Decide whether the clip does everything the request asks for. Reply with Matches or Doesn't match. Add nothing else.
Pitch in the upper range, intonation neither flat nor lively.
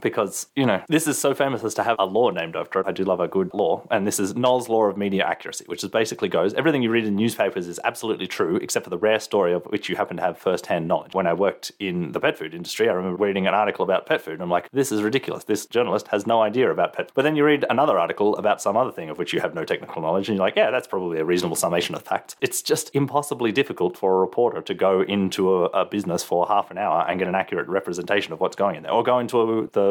Doesn't match